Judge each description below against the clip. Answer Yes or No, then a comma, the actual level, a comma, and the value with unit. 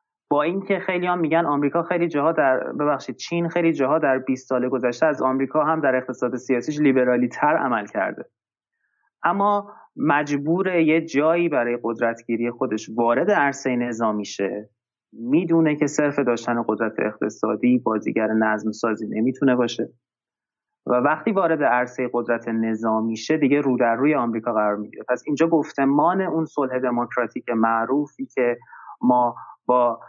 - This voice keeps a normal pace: Yes, average, 145 wpm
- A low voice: Yes, low, 130 Hz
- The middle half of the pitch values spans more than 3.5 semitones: Yes, average, 4.8 semitones